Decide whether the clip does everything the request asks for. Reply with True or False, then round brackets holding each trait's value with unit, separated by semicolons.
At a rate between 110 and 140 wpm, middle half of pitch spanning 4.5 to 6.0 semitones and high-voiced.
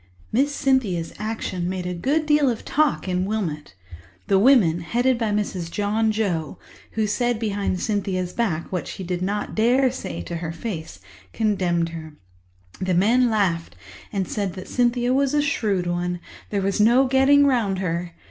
False (160 wpm; 5.2 semitones; 205 Hz)